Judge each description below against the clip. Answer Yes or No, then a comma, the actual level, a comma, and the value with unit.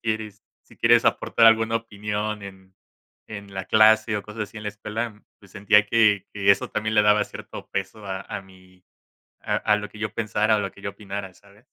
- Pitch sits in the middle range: No, low, 105 Hz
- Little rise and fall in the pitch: Yes, narrow, 1.5 semitones